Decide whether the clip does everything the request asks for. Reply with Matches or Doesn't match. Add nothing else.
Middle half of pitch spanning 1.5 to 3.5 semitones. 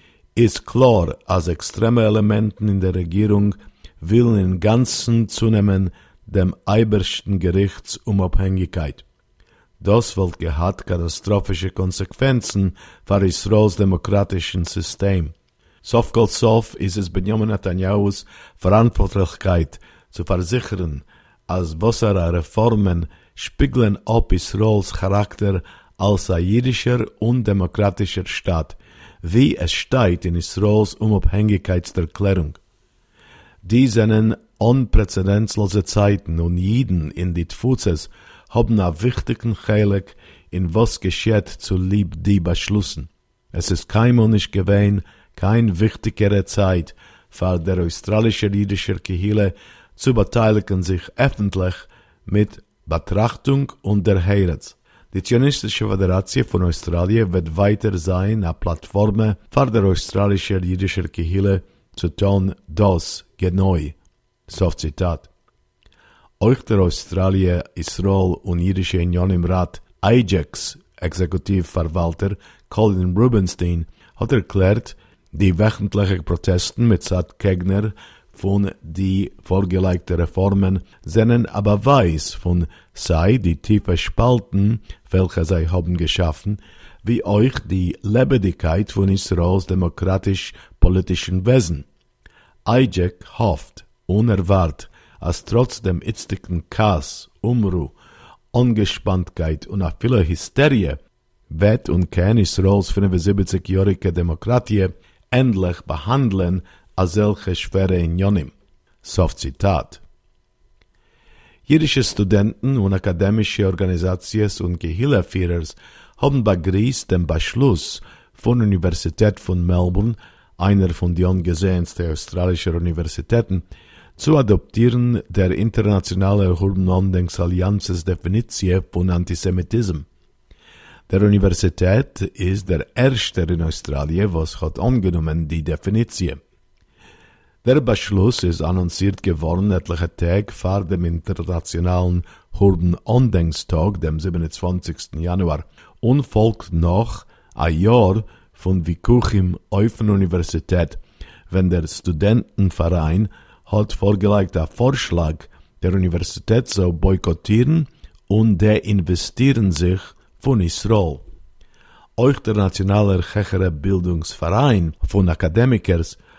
Matches